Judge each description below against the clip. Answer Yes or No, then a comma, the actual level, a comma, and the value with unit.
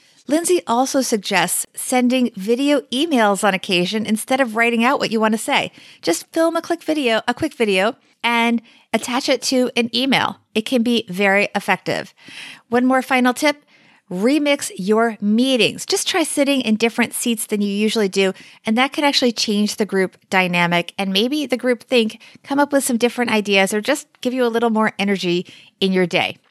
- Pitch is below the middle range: No, high, 235 Hz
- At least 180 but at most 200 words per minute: Yes, average, 190 wpm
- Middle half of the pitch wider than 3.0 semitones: Yes, average, 4.1 semitones